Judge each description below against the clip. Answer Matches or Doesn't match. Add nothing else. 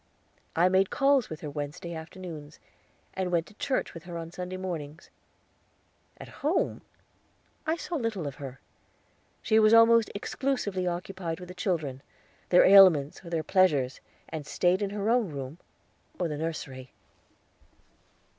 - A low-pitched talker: Doesn't match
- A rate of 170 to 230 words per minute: Doesn't match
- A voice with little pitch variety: Doesn't match